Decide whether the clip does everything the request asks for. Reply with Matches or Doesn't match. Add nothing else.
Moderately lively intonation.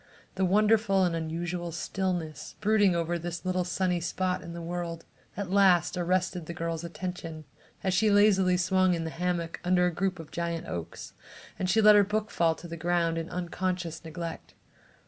Doesn't match